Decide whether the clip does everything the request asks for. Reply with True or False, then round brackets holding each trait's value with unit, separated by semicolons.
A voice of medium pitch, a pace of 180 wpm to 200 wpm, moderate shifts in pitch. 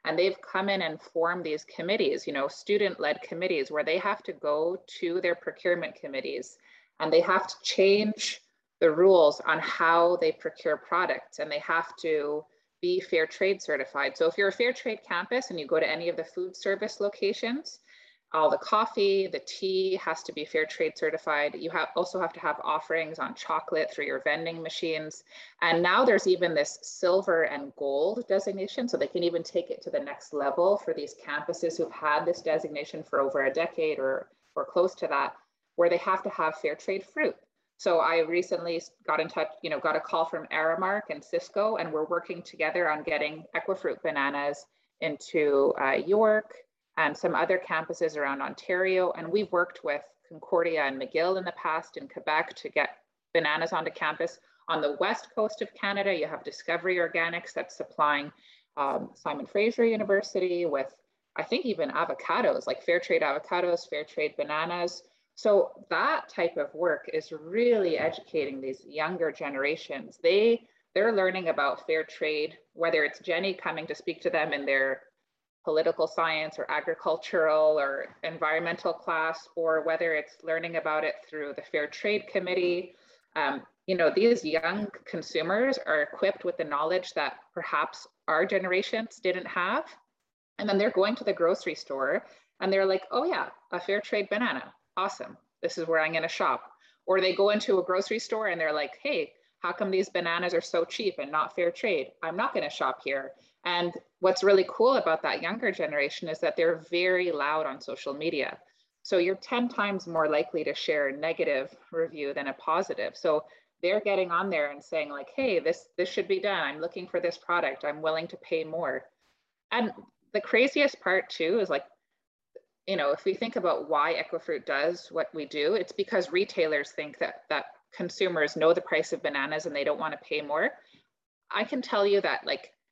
True (175 Hz; 190 wpm; 4.8 semitones)